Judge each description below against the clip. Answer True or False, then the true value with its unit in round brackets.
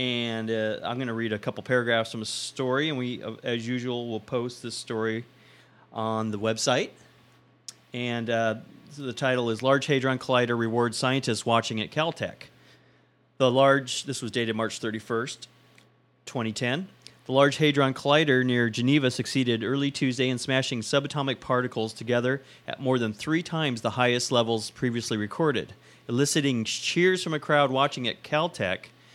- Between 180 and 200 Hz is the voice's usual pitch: False (125 Hz)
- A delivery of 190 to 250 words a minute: False (160 wpm)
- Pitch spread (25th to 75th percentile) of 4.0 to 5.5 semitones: False (2.8 semitones)